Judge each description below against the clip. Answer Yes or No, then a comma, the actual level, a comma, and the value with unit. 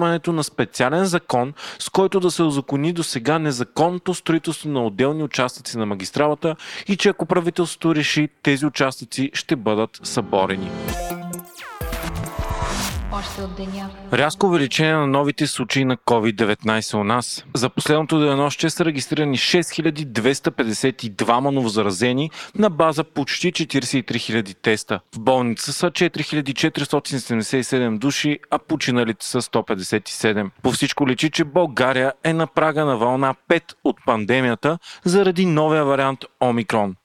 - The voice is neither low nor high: Yes, medium, 145 Hz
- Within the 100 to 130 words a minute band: Yes, average, 125 wpm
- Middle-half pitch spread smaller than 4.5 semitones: No, average, 4.8 semitones